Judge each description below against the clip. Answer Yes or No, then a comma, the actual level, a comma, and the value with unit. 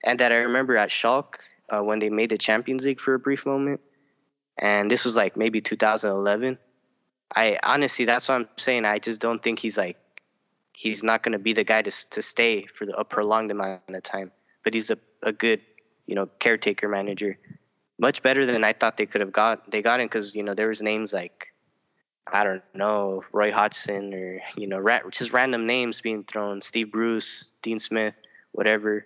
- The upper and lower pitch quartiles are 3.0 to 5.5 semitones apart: No, narrow, 2.6 semitones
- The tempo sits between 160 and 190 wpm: No, fast, 205 wpm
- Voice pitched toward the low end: Yes, low, 110 Hz